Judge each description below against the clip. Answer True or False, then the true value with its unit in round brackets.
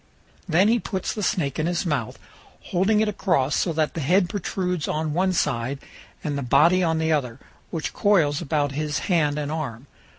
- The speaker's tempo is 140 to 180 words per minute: False (190 wpm)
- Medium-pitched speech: True (160 Hz)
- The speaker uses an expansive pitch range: False (4.1 semitones)